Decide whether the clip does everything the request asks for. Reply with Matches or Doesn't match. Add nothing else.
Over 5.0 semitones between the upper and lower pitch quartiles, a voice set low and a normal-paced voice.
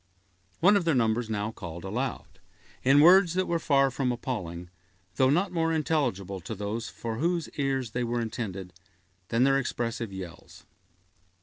Matches